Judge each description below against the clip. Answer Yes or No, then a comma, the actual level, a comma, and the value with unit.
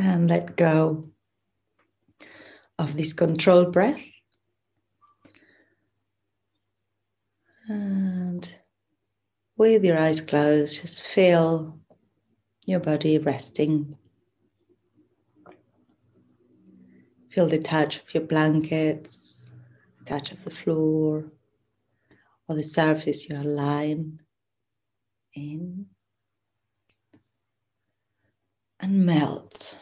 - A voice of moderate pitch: Yes, medium, 145 Hz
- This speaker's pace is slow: Yes, slow, 70 wpm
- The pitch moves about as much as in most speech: No, wide, 7.5 semitones